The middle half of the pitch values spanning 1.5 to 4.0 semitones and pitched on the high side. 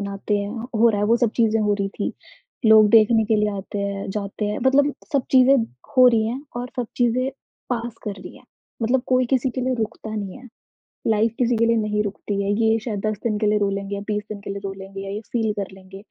Yes: average, 2.9 semitones; high, 215 Hz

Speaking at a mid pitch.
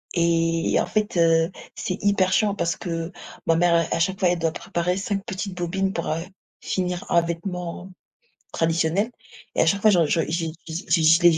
Yes: medium, 175 Hz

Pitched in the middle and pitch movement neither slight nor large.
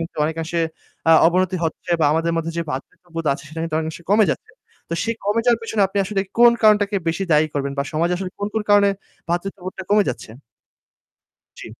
Yes: medium, 180 Hz; average, 4.0 semitones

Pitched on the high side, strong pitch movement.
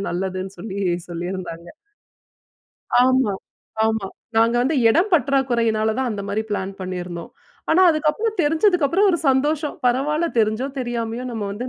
Yes: high, 235 Hz; wide, 6.7 semitones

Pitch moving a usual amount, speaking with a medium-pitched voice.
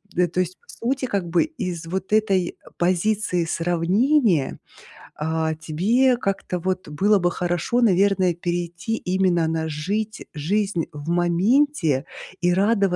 Yes: average, 3.7 semitones; medium, 180 Hz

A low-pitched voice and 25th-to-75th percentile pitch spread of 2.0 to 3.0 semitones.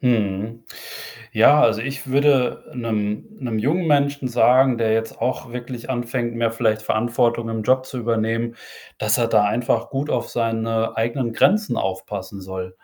Yes: low, 115 Hz; narrow, 2.5 semitones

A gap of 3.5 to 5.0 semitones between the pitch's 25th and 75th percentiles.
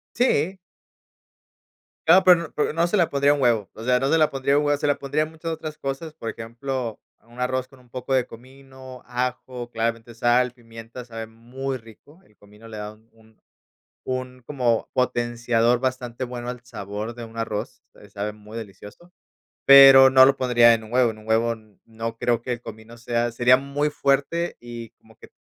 No: average, 3.0 semitones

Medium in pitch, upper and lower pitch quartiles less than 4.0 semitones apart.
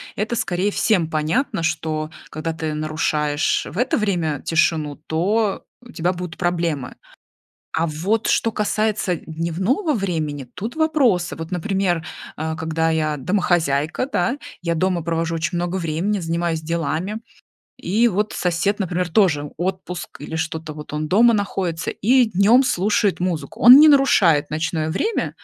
No: medium, 175 Hz; average, 4.4 semitones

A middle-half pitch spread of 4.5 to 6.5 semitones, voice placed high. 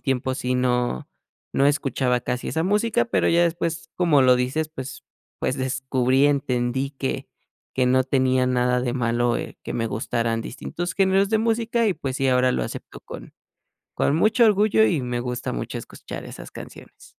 No: average, 5.1 semitones; low, 130 Hz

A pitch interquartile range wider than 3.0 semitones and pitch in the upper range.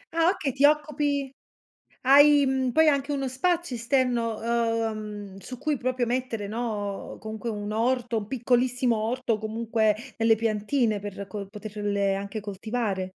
Yes: average, 3.6 semitones; high, 230 Hz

